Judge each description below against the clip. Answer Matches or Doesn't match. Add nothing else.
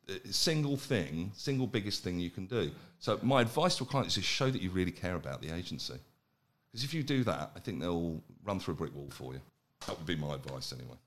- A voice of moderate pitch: Doesn't match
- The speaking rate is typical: Doesn't match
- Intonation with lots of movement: Matches